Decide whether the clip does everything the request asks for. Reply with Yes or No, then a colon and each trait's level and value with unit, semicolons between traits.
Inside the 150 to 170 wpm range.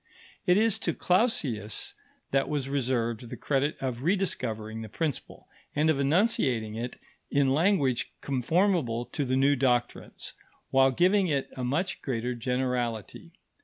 No: slow, 135 wpm